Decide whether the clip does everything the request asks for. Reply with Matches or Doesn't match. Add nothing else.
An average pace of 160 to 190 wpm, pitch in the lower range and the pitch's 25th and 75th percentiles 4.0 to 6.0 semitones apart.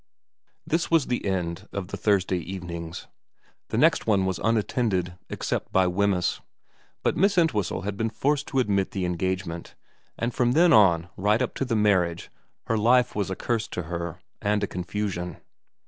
Matches